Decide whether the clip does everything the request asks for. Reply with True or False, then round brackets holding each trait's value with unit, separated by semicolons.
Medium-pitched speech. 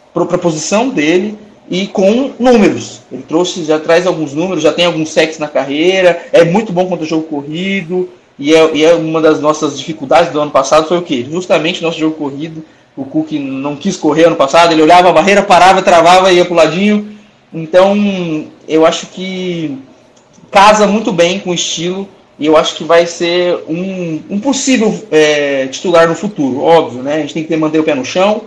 True (170 Hz)